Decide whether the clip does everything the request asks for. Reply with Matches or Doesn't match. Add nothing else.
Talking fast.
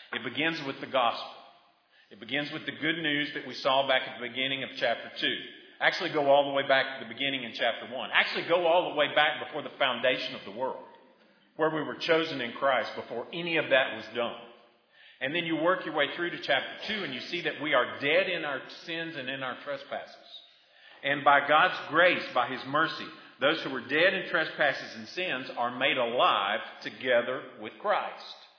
Matches